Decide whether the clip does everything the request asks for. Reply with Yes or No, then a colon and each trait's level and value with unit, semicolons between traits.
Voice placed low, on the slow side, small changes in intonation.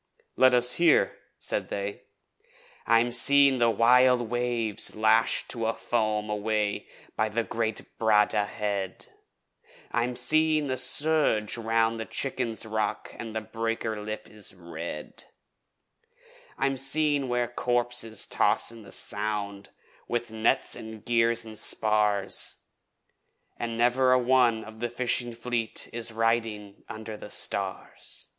Yes: low, 115 Hz; slow, 125 wpm; narrow, 2.2 semitones